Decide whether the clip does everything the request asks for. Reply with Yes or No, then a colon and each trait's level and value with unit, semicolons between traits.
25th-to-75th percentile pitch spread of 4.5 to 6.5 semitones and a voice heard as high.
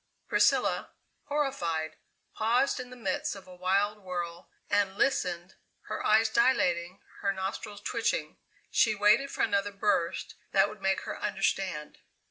No: average, 3.1 semitones; high, 200 Hz